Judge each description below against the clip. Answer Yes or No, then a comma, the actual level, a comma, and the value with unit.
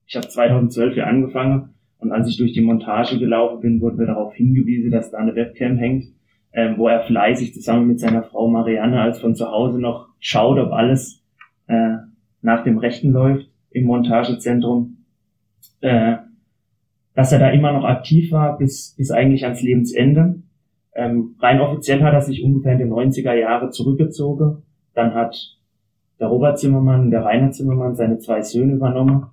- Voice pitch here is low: Yes, low, 120 Hz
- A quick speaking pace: No, average, 170 wpm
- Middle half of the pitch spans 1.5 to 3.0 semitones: Yes, narrow, 2.5 semitones